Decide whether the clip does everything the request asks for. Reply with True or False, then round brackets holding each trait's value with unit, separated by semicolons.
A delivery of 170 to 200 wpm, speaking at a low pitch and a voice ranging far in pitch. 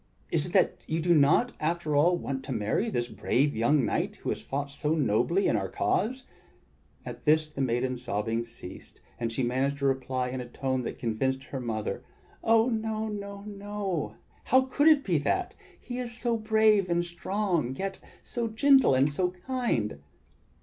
False (180 wpm; 155 Hz; 8.7 semitones)